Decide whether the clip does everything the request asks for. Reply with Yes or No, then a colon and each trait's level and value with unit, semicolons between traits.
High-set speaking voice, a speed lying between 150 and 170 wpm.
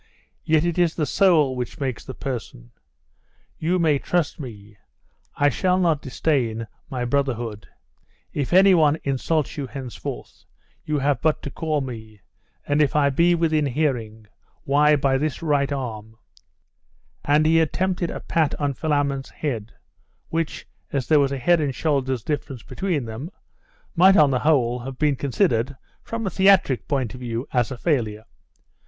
No: medium, 140 Hz; average, 160 wpm